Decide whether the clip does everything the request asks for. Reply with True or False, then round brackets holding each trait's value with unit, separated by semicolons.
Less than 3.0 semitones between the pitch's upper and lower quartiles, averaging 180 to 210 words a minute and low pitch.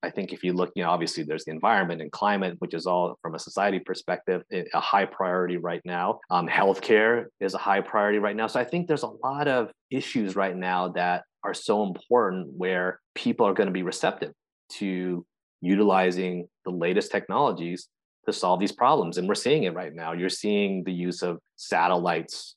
True (2.5 semitones; 200 wpm; 95 Hz)